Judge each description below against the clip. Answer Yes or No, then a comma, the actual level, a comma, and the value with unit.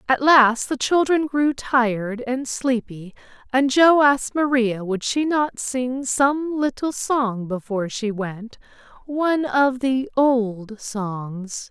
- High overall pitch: Yes, very high, 250 Hz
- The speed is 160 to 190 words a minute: No, average, 140 wpm